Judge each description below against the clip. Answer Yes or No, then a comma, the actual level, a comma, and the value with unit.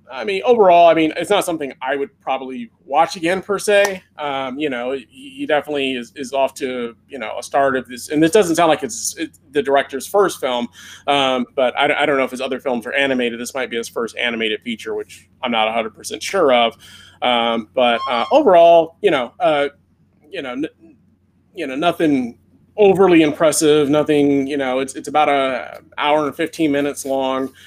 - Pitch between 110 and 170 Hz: Yes, medium, 140 Hz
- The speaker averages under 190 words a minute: No, average, 200 wpm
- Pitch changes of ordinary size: Yes, average, 4.5 semitones